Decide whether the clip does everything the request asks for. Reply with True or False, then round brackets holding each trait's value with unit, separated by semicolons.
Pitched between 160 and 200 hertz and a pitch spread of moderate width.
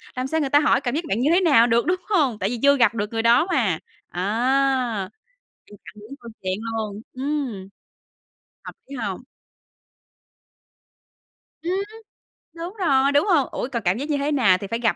False (250 Hz; 4.7 semitones)